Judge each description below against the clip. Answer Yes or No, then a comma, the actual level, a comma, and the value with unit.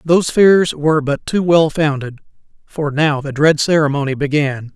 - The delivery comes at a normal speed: Yes, average, 165 wpm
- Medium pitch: Yes, medium, 150 Hz